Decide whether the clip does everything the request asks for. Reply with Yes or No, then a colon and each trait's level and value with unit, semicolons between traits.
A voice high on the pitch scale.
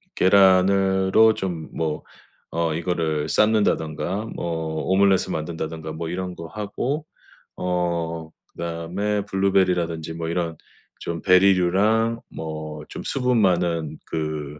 No: very low, 85 Hz